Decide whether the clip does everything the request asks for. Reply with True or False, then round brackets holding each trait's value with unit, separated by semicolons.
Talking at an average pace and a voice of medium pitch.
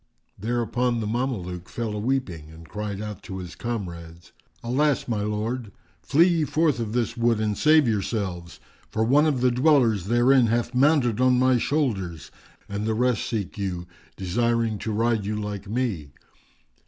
False (165 wpm; 115 Hz)